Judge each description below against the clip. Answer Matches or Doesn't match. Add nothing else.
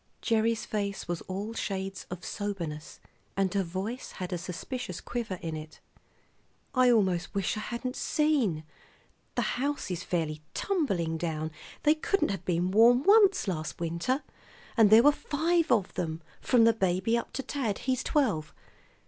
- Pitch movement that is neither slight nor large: Doesn't match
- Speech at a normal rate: Matches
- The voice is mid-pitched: Doesn't match